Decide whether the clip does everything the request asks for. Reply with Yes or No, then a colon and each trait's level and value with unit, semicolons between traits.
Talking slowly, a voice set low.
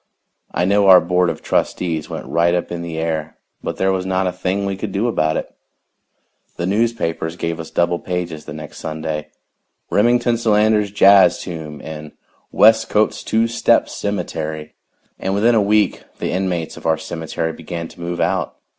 No: average, 175 wpm; very low, 90 Hz